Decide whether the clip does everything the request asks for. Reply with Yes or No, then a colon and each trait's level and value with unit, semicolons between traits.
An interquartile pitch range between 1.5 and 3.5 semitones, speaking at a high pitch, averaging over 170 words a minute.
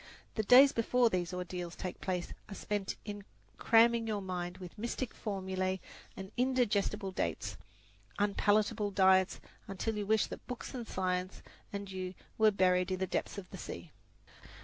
No: average, 2.9 semitones; high, 200 Hz; average, 155 wpm